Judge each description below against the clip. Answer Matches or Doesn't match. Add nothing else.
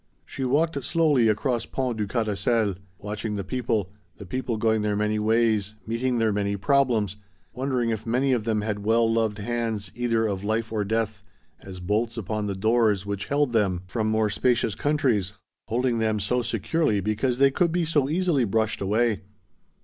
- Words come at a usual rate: Matches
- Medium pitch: Doesn't match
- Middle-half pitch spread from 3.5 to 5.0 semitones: Doesn't match